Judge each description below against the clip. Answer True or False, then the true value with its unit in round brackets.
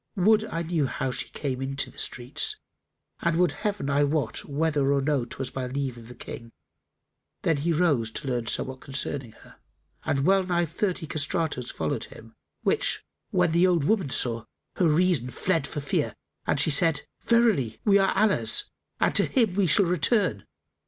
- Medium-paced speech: True (180 wpm)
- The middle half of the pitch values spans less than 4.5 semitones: False (5.2 semitones)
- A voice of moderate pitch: True (150 Hz)